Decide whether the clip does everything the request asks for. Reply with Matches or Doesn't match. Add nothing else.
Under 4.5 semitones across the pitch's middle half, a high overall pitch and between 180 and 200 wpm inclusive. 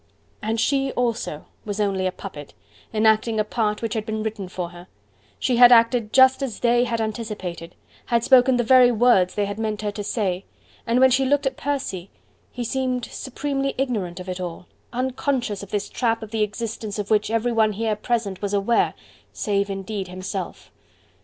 Matches